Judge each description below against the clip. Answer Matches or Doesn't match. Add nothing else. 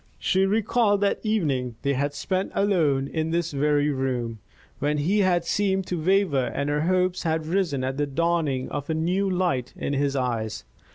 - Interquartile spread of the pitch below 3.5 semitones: Doesn't match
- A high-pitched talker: Doesn't match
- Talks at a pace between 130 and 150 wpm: Doesn't match